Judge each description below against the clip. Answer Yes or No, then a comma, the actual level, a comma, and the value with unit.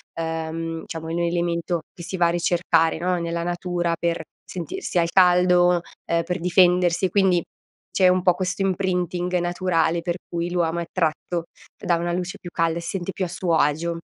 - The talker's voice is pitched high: No, medium, 175 Hz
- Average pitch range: No, narrow, 1.2 semitones